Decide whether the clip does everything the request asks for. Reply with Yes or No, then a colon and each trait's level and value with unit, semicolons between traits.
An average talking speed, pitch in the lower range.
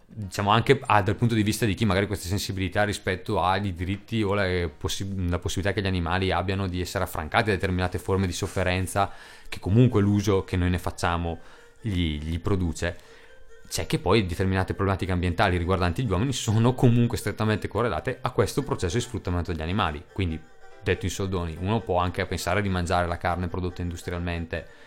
No: fast, 185 wpm; very low, 95 Hz